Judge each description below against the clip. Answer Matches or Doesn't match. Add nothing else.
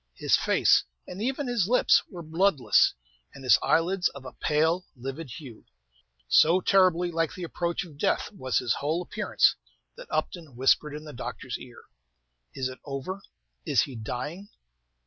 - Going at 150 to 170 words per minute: Matches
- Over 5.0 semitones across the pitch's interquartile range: Matches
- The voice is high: Doesn't match